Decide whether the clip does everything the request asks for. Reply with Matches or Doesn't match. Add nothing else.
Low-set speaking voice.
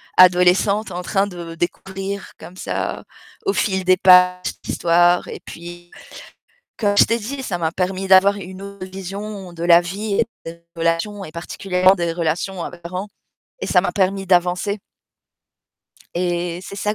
Doesn't match